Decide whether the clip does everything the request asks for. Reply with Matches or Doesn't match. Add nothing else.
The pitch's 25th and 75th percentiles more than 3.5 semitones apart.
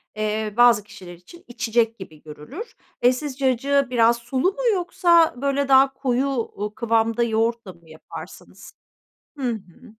Matches